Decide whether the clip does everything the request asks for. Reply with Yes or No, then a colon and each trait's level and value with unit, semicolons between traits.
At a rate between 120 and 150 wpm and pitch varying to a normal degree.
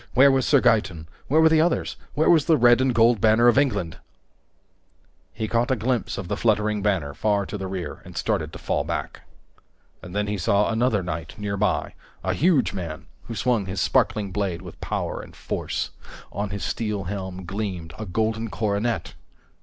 No: average, 185 wpm; average, 4.0 semitones